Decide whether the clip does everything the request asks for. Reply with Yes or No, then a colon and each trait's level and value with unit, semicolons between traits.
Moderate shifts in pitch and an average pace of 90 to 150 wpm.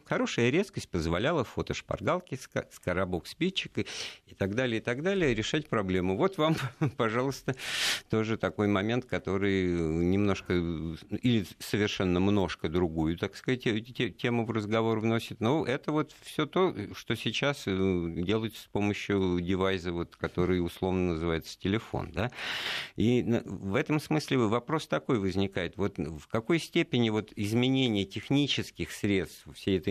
Yes: average, 5.0 semitones; average, 130 wpm